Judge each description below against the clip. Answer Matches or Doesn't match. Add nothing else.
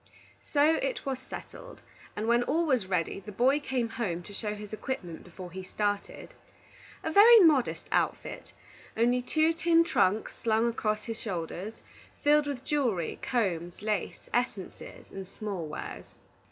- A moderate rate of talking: Matches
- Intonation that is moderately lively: Doesn't match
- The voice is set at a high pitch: Matches